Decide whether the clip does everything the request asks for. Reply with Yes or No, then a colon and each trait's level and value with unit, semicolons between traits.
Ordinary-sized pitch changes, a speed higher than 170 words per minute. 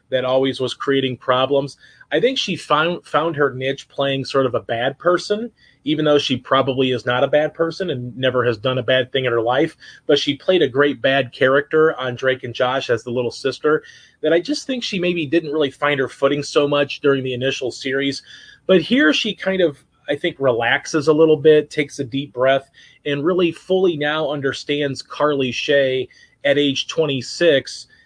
Yes: average, 3.4 semitones; average, 200 wpm